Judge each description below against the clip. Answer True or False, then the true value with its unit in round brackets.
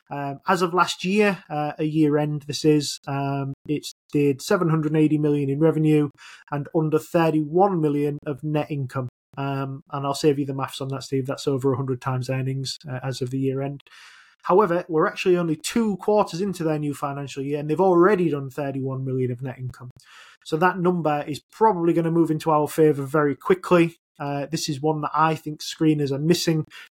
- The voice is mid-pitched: True (150 Hz)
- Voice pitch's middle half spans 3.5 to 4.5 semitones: False (2.9 semitones)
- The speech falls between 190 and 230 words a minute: True (200 wpm)